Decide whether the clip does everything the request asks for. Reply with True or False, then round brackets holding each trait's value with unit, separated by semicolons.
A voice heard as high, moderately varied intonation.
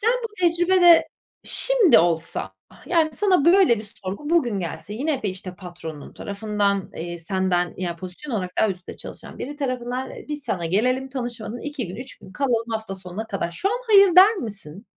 False (225 Hz; 8.2 semitones)